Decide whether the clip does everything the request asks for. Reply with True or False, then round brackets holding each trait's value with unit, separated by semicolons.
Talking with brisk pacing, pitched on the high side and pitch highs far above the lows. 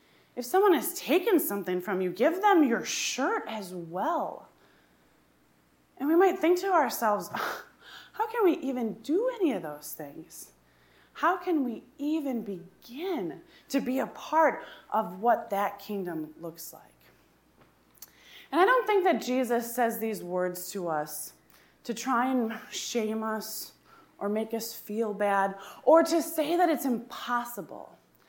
False (150 wpm; 240 Hz; 8.2 semitones)